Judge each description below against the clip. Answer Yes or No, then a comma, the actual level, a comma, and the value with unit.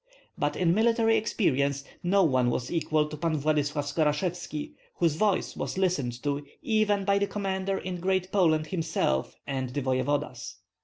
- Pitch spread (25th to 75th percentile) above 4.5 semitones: Yes, average, 5.0 semitones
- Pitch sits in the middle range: Yes, medium, 160 Hz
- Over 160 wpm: No, average, 155 wpm